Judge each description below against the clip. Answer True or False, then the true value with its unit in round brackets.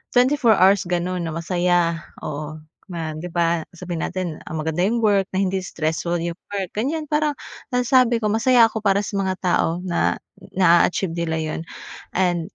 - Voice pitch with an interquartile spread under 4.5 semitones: True (3.7 semitones)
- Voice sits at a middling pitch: True (180 Hz)